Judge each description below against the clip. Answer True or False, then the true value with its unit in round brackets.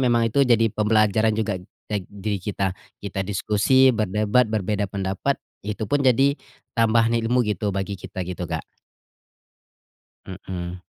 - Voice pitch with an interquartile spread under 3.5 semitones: True (2.8 semitones)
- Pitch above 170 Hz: False (105 Hz)